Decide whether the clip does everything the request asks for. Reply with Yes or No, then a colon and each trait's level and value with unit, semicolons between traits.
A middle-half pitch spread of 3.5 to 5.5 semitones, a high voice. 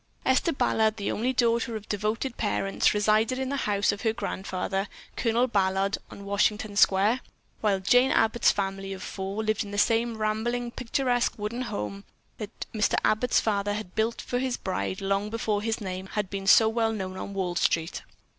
No: average, 2.8 semitones; high, 215 Hz